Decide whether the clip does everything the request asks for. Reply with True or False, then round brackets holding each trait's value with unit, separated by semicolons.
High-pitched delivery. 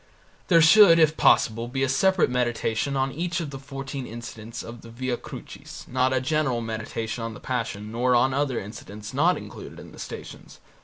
False (130 Hz)